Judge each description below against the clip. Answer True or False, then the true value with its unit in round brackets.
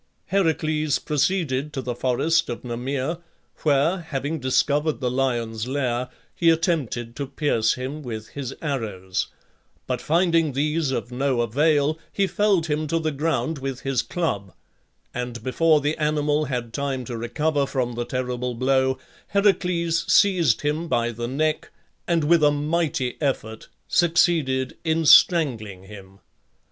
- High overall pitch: False (140 Hz)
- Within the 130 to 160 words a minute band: True (140 wpm)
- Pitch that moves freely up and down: False (4.4 semitones)